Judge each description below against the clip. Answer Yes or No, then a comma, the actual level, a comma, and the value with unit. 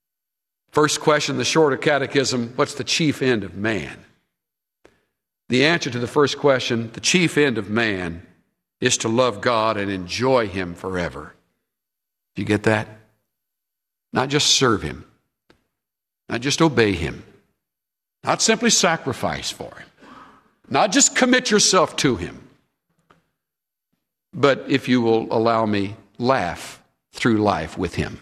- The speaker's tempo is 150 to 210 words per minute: No, slow, 135 wpm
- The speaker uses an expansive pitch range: Yes, wide, 5.9 semitones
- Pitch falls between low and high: No, low, 120 Hz